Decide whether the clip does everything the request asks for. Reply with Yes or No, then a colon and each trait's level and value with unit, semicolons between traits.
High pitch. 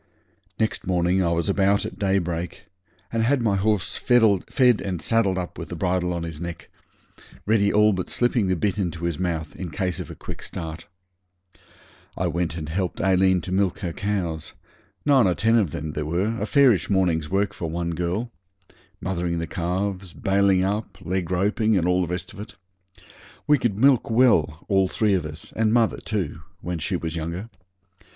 No: very low, 95 Hz